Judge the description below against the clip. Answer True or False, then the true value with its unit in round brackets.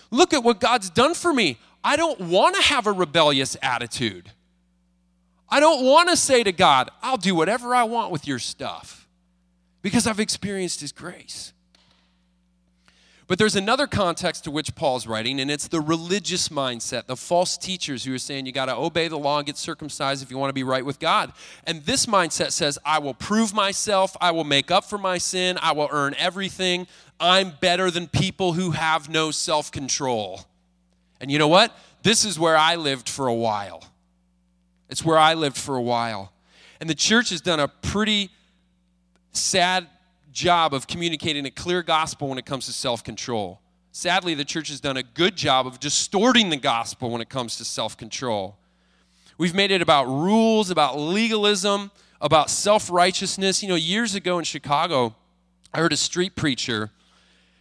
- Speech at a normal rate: True (180 wpm)